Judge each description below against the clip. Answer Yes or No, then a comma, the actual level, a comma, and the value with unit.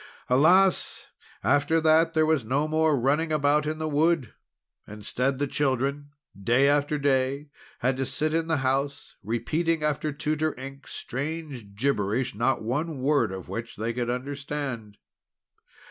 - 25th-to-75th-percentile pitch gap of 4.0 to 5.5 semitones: No, average, 3.5 semitones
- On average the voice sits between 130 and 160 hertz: Yes, medium, 140 Hz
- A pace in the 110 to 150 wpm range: Yes, average, 145 wpm